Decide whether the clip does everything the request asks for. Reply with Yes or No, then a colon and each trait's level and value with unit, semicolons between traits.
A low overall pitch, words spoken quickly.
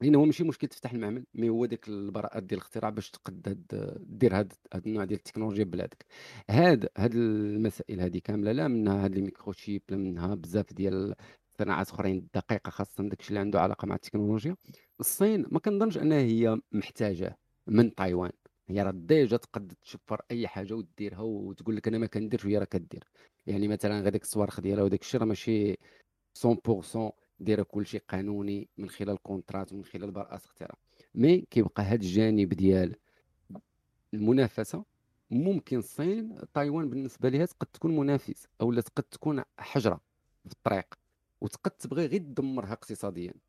Yes: low, 105 Hz; fast, 155 wpm